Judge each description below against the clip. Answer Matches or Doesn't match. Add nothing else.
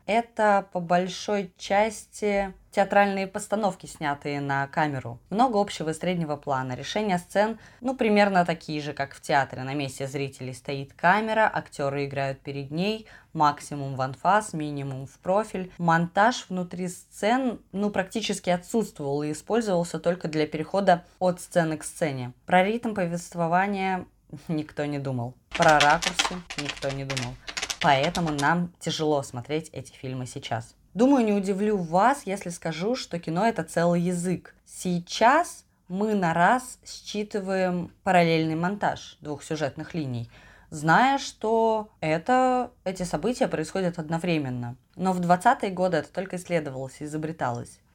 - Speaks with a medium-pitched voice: Matches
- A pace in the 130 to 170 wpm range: Matches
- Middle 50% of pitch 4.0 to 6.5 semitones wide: Matches